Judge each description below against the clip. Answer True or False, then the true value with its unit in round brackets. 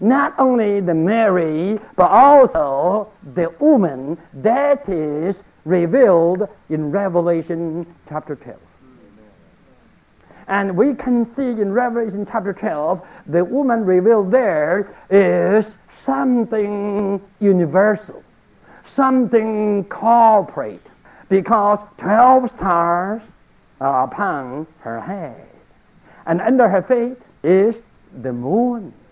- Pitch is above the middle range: True (205 Hz)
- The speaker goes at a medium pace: False (95 wpm)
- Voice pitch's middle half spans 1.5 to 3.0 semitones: False (5.1 semitones)